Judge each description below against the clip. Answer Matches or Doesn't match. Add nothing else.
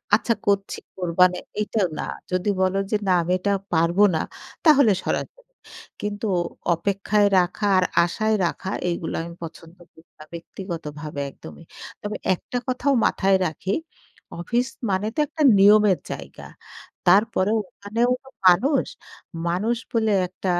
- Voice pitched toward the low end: Doesn't match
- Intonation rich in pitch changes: Doesn't match